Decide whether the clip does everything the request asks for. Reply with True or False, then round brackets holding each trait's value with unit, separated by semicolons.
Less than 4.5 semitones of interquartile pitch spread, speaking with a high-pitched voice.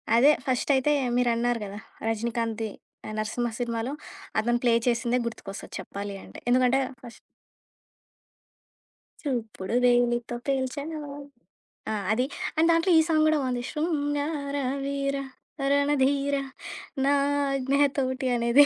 True (3.1 semitones; 255 Hz)